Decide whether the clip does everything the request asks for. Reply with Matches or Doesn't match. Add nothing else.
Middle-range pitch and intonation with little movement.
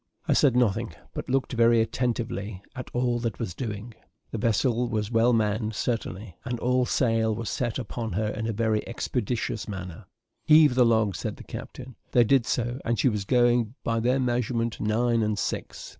Doesn't match